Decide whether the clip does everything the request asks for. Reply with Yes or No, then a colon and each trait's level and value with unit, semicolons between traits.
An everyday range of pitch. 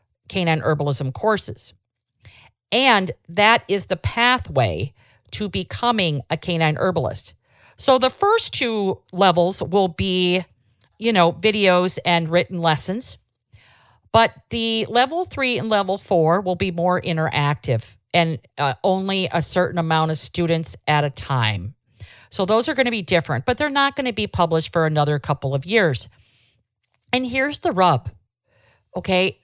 No: wide, 7.5 semitones